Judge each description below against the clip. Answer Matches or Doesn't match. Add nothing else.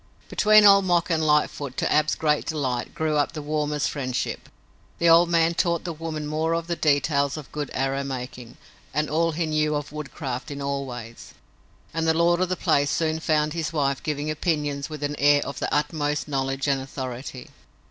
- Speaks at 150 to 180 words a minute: Doesn't match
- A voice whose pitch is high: Doesn't match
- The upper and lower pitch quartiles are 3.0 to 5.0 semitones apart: Doesn't match